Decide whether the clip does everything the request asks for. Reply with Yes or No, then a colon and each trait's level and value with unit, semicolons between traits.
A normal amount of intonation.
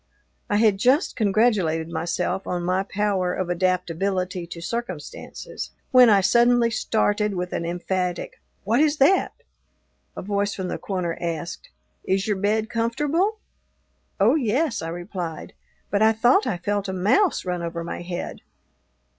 Yes: average, 4.3 semitones